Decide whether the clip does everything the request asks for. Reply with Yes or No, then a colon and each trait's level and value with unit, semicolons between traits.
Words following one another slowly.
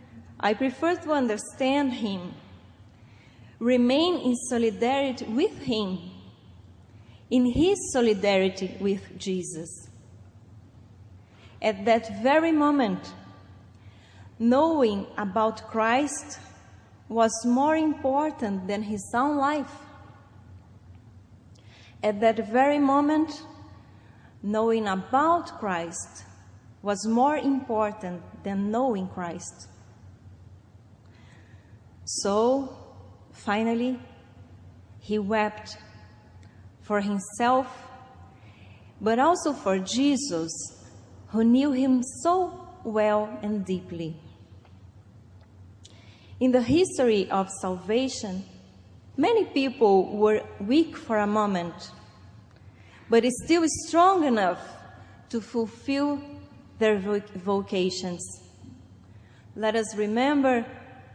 Yes: slow, 80 wpm